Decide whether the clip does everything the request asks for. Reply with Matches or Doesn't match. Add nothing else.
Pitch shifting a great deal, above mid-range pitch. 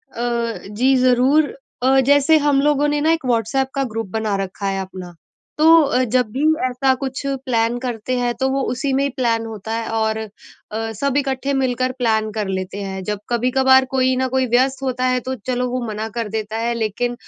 Doesn't match